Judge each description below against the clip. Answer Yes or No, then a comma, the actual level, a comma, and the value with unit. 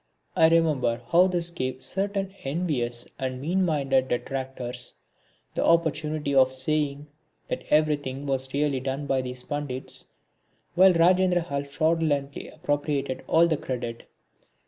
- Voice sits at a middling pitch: Yes, medium, 145 Hz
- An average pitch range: Yes, average, 3.9 semitones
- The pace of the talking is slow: Yes, slow, 125 wpm